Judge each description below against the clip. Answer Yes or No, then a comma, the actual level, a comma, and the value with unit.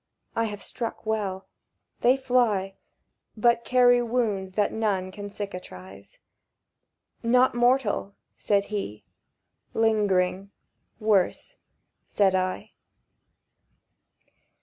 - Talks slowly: Yes, slow, 80 wpm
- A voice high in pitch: Yes, high, 210 Hz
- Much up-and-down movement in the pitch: No, average, 3.6 semitones